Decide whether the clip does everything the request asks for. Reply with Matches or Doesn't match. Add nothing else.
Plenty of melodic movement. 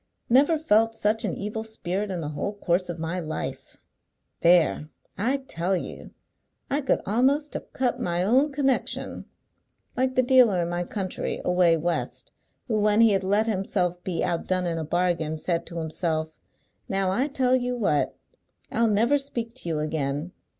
Matches